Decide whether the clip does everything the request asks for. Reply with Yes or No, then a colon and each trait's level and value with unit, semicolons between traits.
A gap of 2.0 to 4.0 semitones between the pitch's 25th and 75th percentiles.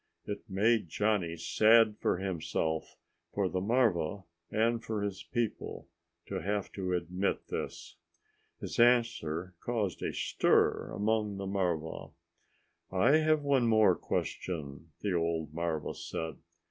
No: average, 4.6 semitones